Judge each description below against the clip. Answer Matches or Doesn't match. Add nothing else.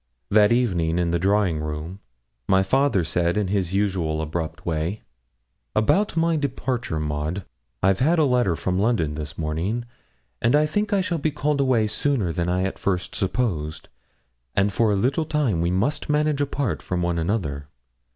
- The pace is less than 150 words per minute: Doesn't match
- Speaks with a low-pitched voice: Matches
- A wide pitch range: Matches